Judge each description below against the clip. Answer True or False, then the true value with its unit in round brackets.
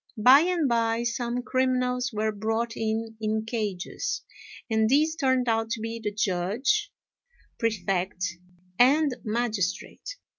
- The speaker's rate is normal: False (120 wpm)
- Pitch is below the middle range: False (230 Hz)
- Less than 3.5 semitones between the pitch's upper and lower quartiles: True (2.9 semitones)